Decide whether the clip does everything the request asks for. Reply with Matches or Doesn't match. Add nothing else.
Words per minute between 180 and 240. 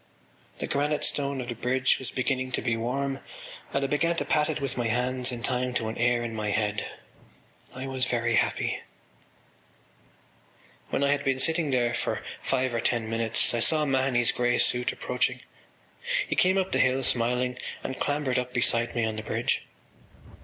Matches